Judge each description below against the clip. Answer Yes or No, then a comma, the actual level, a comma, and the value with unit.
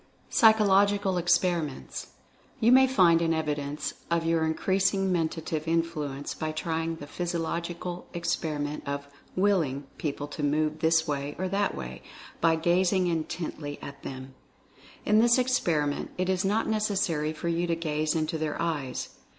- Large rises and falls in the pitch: No, average, 3.3 semitones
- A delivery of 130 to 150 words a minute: Yes, average, 145 wpm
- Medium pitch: Yes, medium, 165 Hz